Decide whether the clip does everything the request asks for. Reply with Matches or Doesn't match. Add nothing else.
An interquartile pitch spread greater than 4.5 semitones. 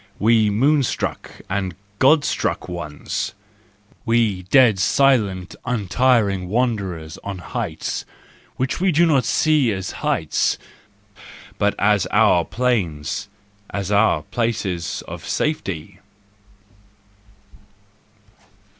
Matches